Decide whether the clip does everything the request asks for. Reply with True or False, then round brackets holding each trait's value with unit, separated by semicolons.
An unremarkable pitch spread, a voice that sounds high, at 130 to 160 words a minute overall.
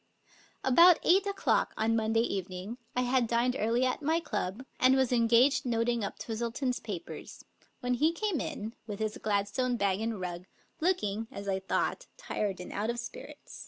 False (3.8 semitones; 235 Hz; 175 wpm)